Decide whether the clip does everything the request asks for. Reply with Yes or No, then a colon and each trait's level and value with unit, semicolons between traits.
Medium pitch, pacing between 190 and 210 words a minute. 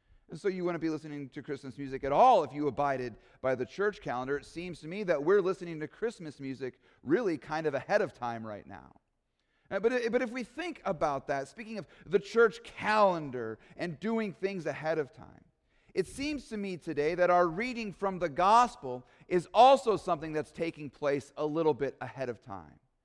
Yes: medium, 160 Hz; average, 195 wpm